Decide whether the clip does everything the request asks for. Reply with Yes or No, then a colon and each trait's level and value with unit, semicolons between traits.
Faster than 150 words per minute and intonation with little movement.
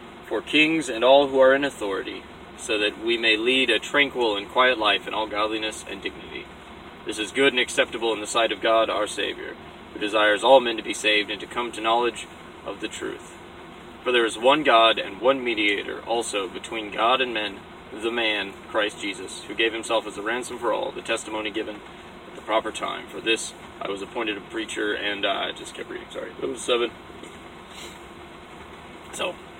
No: average, 200 wpm; average, 3.0 semitones